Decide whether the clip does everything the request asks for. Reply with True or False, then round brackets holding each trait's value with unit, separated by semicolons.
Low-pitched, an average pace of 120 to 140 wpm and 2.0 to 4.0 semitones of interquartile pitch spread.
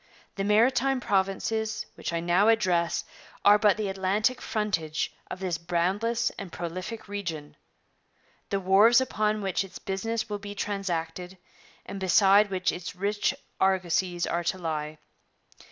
False (195 Hz; 135 wpm; 3.1 semitones)